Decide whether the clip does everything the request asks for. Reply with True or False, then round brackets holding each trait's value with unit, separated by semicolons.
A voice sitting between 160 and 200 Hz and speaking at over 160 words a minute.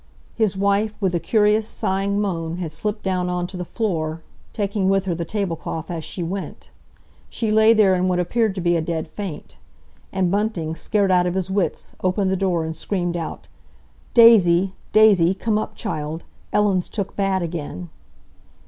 True (190 Hz; 175 wpm)